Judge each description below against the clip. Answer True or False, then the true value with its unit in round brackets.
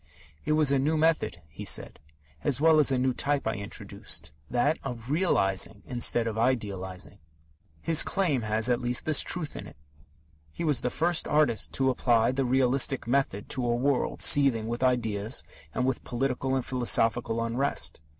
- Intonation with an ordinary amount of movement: True (3.6 semitones)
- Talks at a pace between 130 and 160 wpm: False (170 wpm)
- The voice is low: True (125 Hz)